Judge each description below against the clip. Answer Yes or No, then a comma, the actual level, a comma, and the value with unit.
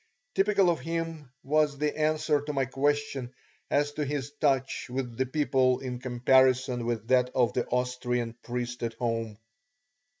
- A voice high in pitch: No, low, 130 Hz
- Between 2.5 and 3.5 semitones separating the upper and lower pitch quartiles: Yes, average, 3.1 semitones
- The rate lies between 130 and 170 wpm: Yes, average, 155 wpm